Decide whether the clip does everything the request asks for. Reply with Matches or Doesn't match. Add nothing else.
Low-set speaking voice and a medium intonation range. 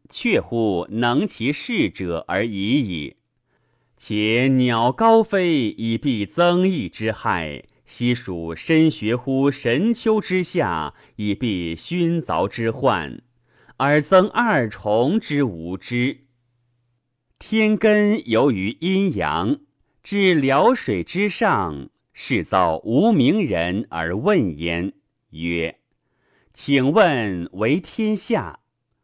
Doesn't match